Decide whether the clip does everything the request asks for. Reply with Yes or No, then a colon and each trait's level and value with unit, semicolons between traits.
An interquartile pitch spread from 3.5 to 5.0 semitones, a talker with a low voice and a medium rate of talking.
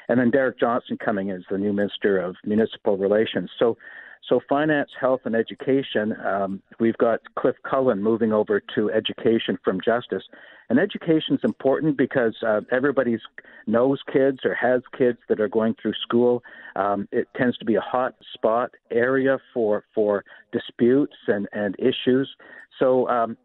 Yes: average, 3.9 semitones; low, 120 Hz; average, 165 wpm